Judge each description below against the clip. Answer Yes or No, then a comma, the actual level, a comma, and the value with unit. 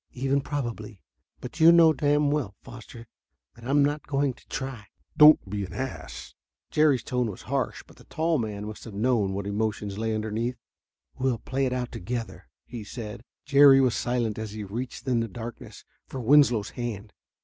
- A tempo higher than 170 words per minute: Yes, average, 180 wpm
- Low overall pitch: Yes, low, 120 Hz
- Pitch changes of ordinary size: Yes, average, 4.0 semitones